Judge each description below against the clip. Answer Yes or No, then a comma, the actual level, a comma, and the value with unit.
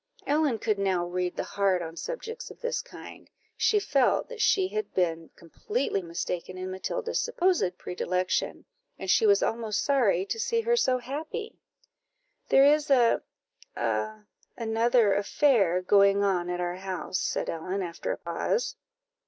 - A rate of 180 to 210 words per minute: No, average, 155 wpm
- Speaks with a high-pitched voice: Yes, high, 215 Hz